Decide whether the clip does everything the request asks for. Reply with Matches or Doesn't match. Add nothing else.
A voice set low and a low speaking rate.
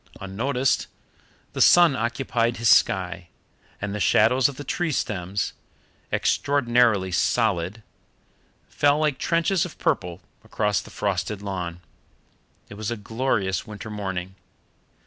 Matches